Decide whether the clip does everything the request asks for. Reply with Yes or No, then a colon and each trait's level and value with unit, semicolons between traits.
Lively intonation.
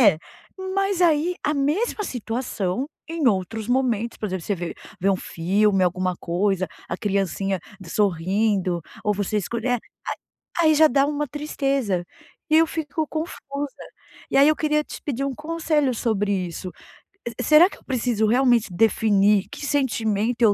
Yes: wide, 6.8 semitones